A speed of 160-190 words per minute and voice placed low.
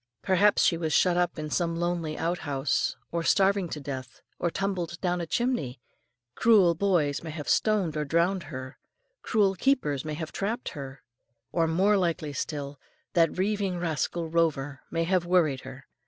No: average, 170 wpm; medium, 170 Hz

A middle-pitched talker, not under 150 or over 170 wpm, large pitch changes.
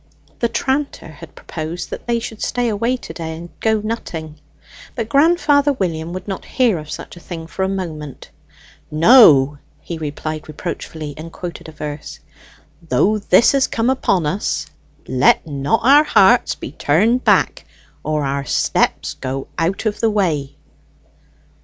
Yes: medium, 175 Hz; average, 155 wpm; wide, 6.9 semitones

